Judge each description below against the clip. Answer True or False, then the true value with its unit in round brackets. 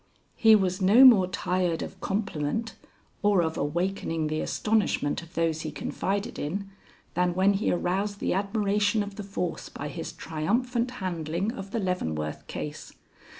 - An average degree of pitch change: True (3.6 semitones)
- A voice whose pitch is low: False (190 Hz)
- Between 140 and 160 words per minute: True (150 wpm)